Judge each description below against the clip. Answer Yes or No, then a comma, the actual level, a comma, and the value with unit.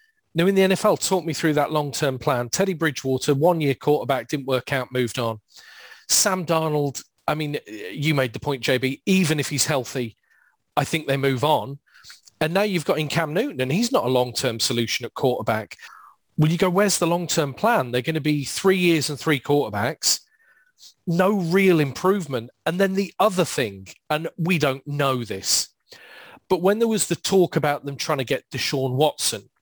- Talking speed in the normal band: Yes, average, 190 wpm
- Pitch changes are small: No, average, 5.2 semitones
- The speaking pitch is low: No, medium, 150 Hz